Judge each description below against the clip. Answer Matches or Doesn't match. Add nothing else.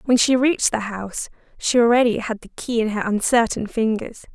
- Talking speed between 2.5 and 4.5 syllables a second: Doesn't match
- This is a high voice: Matches